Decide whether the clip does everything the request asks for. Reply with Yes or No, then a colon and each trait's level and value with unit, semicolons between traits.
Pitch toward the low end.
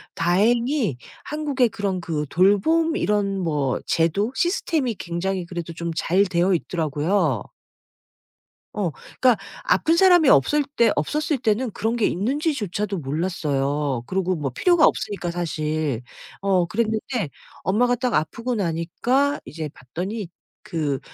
No: high, 190 Hz